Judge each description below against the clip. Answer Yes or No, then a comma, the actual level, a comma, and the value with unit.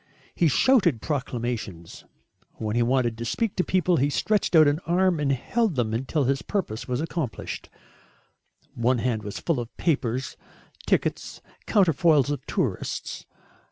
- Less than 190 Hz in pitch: Yes, medium, 140 Hz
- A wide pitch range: Yes, wide, 6.1 semitones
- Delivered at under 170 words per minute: Yes, average, 145 wpm